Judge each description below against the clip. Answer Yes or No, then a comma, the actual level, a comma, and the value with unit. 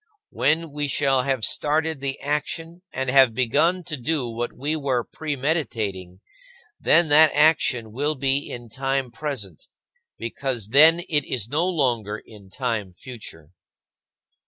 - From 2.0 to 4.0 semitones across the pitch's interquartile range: No, average, 4.4 semitones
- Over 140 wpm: No, slow, 135 wpm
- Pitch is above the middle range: No, low, 135 Hz